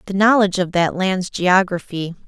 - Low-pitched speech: No, medium, 185 Hz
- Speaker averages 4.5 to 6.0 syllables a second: Yes, 5.0 syllables/s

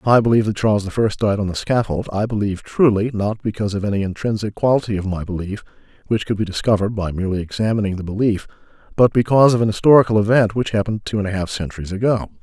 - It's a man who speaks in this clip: Yes, male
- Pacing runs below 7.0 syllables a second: No, 7.2 syllables/s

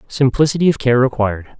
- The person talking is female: No, male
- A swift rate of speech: No, average, 150 wpm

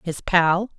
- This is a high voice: No, medium, 180 Hz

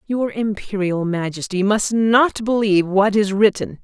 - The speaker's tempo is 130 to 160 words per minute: Yes, average, 140 wpm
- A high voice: Yes, high, 205 Hz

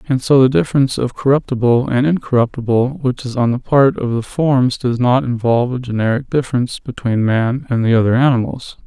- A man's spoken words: Yes, male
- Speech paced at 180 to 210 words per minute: Yes, average, 190 wpm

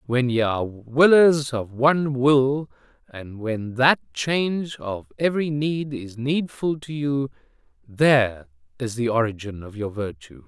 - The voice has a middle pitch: No, low, 125 Hz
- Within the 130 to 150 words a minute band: Yes, average, 145 wpm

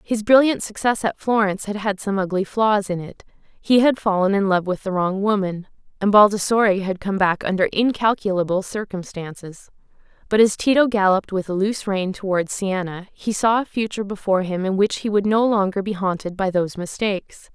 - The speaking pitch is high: Yes, high, 200 Hz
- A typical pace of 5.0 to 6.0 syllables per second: Yes, 5.5 syllables/s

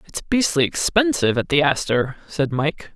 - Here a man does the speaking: No, female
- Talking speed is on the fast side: No, average, 165 wpm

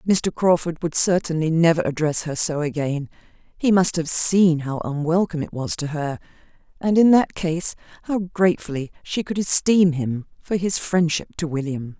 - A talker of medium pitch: Yes, medium, 165 Hz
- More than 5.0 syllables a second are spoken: No, 4.9 syllables/s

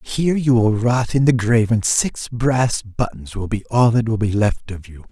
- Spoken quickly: Yes, fast, 235 wpm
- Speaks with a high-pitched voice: No, low, 115 Hz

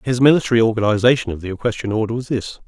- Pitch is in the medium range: No, low, 115 Hz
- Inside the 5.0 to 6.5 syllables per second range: No, 7.5 syllables/s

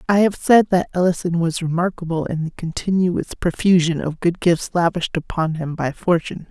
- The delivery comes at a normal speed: Yes, average, 175 wpm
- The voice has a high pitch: No, medium, 170 Hz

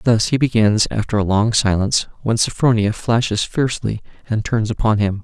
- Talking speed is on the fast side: No, average, 170 wpm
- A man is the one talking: Yes, male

